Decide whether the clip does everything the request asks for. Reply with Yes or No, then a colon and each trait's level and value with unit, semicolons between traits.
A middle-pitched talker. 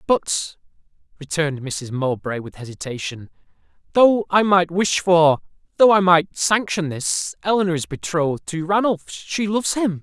Yes: medium, 170 Hz